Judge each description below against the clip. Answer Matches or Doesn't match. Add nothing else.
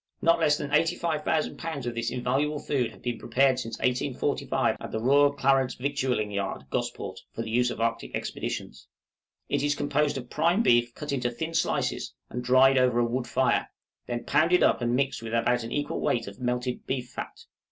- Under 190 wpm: Doesn't match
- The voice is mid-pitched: Doesn't match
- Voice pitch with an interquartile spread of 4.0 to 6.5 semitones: Doesn't match